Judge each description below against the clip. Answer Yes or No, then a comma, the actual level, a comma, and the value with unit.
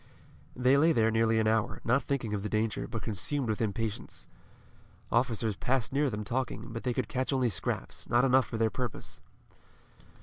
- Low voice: Yes, low, 115 Hz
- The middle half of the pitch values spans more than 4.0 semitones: No, average, 2.8 semitones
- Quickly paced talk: No, average, 180 wpm